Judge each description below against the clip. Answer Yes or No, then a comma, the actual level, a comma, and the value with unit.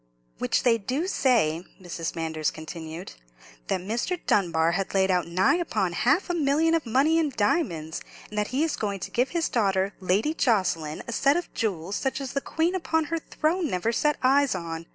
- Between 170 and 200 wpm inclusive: Yes, average, 195 wpm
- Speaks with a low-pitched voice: No, high, 220 Hz